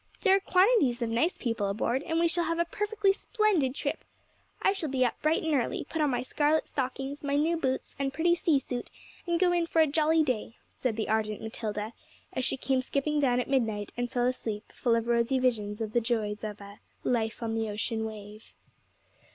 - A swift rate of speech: Yes, fast, 215 wpm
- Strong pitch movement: Yes, wide, 6.1 semitones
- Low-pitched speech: No, very high, 255 Hz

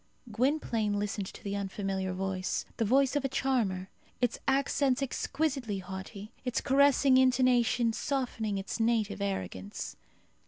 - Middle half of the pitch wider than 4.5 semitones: Yes, average, 5.0 semitones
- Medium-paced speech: No, slow, 125 wpm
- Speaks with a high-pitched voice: Yes, high, 225 Hz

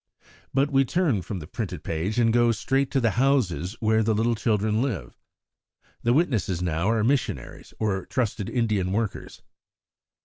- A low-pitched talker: Yes, low, 110 Hz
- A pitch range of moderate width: Yes, average, 4.2 semitones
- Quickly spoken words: No, average, 160 wpm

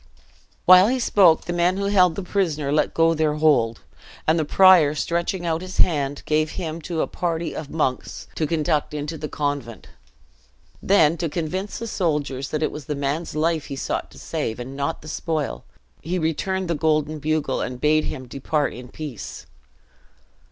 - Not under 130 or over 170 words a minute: No, average, 180 wpm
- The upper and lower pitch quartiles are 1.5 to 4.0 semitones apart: Yes, average, 2.9 semitones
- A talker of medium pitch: Yes, medium, 155 Hz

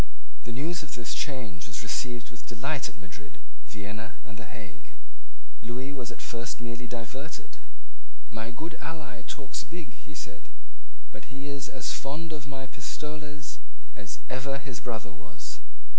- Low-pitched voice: Yes, low, 125 Hz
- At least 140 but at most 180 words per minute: Yes, average, 155 wpm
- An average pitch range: Yes, average, 4.2 semitones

